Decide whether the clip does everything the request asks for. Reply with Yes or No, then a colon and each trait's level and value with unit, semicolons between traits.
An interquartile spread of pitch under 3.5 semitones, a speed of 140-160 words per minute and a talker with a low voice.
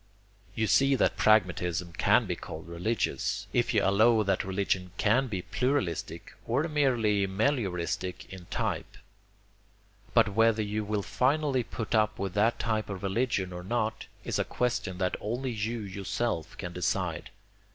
No: average, 4.2 semitones; average, 150 wpm; low, 105 Hz